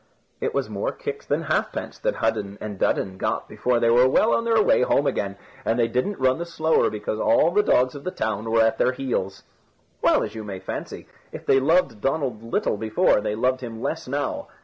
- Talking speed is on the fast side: Yes, fast, 215 wpm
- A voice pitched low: Yes, low, 125 Hz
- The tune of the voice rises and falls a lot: Yes, wide, 5.8 semitones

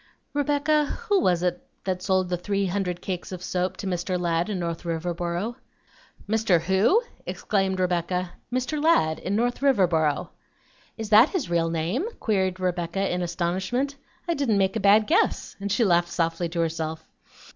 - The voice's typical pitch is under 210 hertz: Yes, medium, 185 Hz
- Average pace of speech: Yes, average, 165 wpm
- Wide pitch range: No, average, 3.9 semitones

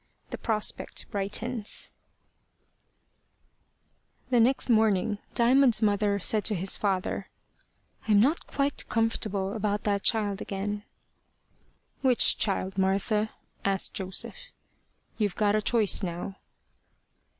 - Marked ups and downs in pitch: No, narrow, 2.4 semitones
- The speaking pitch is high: Yes, high, 210 Hz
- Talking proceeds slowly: Yes, slow, 105 wpm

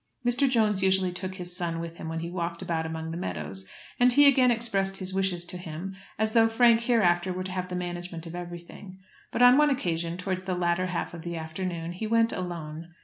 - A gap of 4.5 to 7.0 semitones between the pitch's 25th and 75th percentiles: No, average, 3.2 semitones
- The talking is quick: Yes, fast, 220 wpm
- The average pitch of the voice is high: No, medium, 180 Hz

